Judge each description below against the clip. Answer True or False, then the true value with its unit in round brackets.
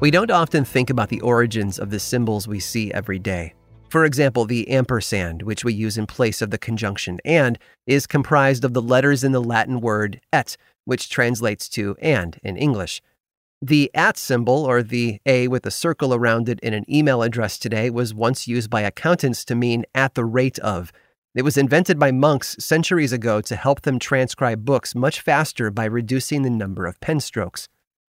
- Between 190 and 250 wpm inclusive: True (195 wpm)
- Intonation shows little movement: False (3.8 semitones)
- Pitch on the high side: False (120 Hz)